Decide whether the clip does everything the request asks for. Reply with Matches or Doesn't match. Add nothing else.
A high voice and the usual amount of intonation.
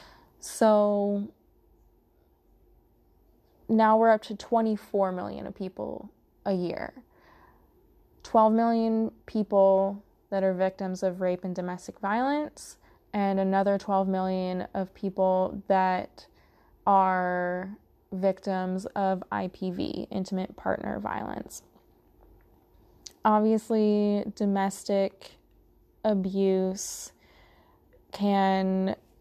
Doesn't match